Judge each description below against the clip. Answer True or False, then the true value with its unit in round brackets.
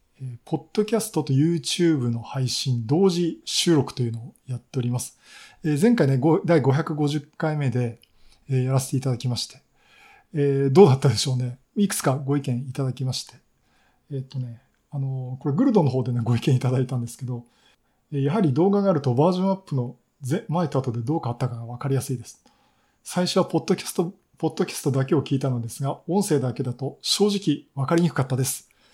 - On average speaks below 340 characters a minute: False (410 characters per minute)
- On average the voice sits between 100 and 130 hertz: False (140 Hz)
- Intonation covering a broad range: False (4.3 semitones)